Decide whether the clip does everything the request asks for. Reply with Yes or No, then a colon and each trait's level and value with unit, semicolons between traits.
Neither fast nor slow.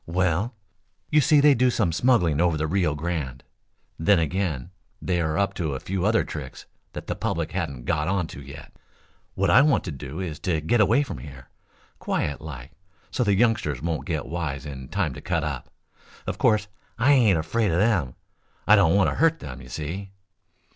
Yes: average, 195 wpm